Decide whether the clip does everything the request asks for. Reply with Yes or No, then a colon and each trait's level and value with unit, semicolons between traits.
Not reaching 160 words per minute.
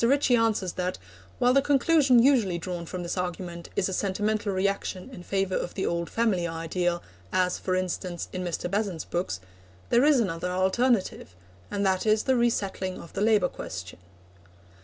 No: average, 170 wpm